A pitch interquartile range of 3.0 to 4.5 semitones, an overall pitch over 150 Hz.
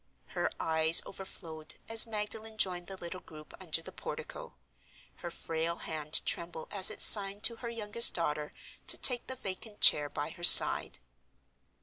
No: average, 5.2 semitones; medium, 185 Hz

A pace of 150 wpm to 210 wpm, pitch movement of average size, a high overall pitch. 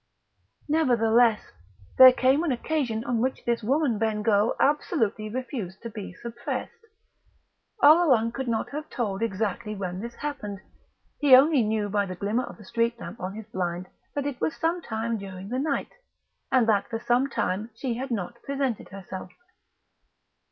Yes: average, 160 wpm; average, 4.0 semitones; high, 230 Hz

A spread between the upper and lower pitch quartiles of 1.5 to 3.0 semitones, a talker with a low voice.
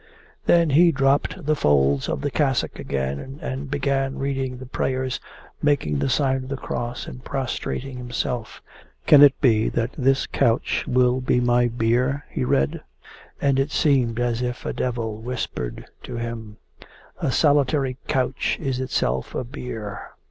Yes: narrow, 2.6 semitones; low, 130 Hz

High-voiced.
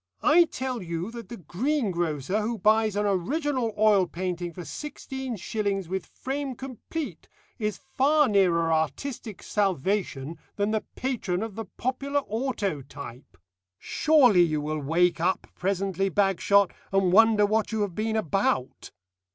Yes: high, 205 Hz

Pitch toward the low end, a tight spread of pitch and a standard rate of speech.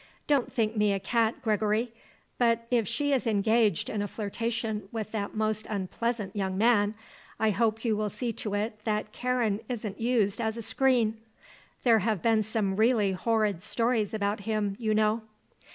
No: high, 220 Hz; narrow, 1.9 semitones; average, 170 wpm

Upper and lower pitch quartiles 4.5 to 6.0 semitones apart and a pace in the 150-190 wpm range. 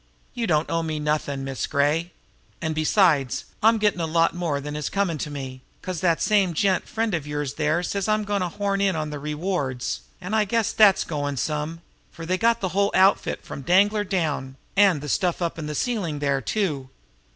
No: average, 4.9 semitones; fast, 205 wpm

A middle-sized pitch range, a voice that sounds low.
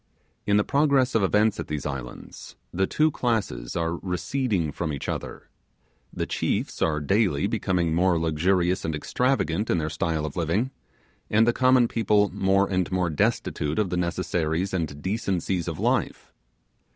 Yes: average, 4.7 semitones; very low, 90 Hz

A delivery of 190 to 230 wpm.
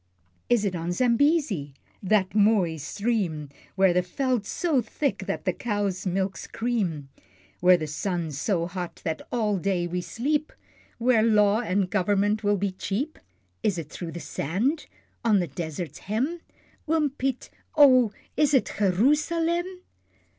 No: average, 150 wpm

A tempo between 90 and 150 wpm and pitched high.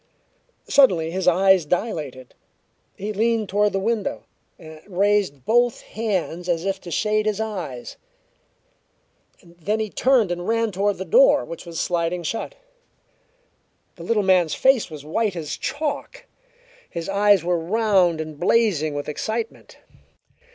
Yes: slow, 135 wpm; high, 195 Hz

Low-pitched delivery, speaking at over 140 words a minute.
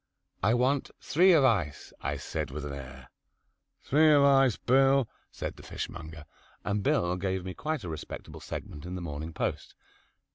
Yes: very low, 95 Hz; average, 170 wpm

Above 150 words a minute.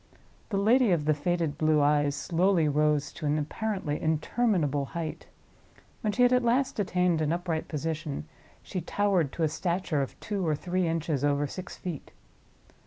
Yes: average, 170 wpm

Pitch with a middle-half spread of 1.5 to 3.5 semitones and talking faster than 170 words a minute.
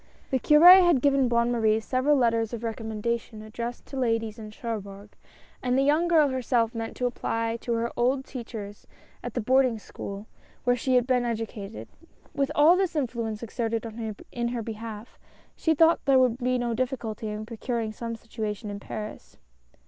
Yes: average, 2.7 semitones; average, 180 wpm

